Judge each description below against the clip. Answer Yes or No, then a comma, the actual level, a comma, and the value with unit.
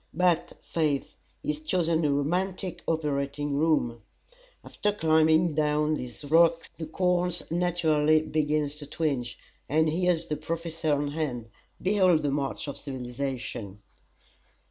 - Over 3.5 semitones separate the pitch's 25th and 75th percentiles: No, average, 2.7 semitones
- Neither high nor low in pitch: Yes, medium, 155 Hz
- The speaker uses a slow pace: Yes, slow, 120 wpm